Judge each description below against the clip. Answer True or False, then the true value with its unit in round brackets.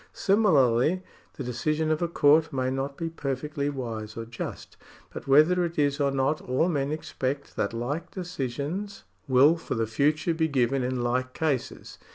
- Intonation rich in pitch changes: False (3.7 semitones)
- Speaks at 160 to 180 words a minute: True (170 wpm)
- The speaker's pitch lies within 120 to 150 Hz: True (140 Hz)